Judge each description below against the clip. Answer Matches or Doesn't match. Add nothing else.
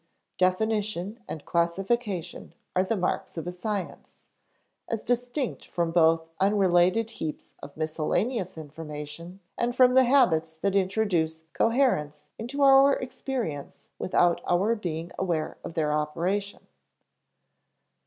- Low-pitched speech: Doesn't match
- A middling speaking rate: Doesn't match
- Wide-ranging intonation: Matches